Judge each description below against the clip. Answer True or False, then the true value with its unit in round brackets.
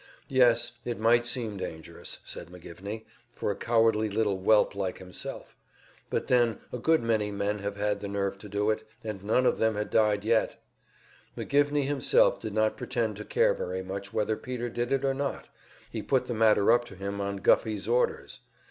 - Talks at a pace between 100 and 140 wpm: False (190 wpm)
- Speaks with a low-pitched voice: True (110 Hz)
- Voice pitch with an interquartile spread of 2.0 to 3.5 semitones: True (2.9 semitones)